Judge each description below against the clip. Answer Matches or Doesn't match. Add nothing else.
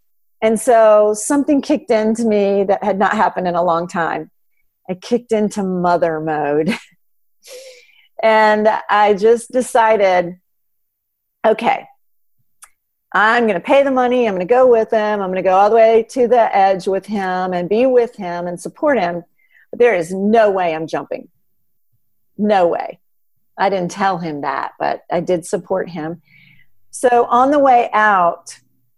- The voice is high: Matches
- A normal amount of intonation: Matches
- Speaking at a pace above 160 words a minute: Doesn't match